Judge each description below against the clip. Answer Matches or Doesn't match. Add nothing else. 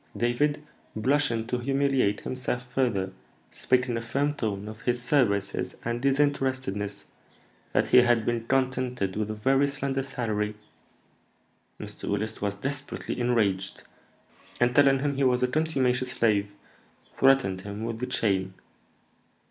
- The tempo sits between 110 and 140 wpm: Matches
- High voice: Doesn't match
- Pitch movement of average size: Matches